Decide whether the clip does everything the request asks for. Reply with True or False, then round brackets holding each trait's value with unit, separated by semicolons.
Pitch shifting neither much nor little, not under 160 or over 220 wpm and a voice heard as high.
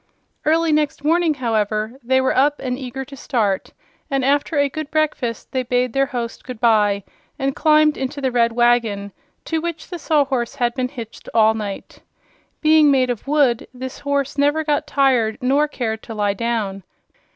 True (3.8 semitones; 175 wpm; 260 Hz)